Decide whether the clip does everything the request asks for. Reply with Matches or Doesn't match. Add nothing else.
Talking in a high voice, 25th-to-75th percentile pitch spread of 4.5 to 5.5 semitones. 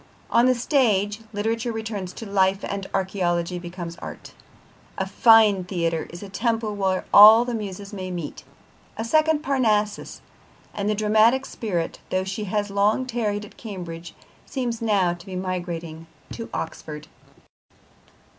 Doesn't match